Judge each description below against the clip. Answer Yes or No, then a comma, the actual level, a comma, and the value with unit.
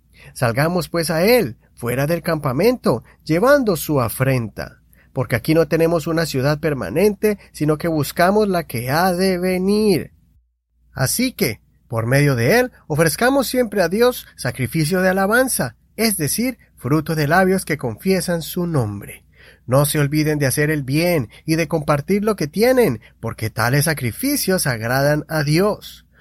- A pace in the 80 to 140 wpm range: No, average, 150 wpm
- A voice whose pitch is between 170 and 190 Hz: No, medium, 160 Hz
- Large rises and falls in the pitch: Yes, wide, 6.3 semitones